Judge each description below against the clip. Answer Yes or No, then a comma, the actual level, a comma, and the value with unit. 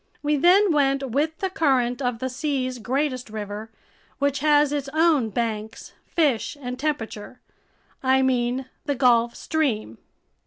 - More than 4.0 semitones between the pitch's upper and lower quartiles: No, average, 3.5 semitones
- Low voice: No, very high, 265 Hz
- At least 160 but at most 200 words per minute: No, average, 140 wpm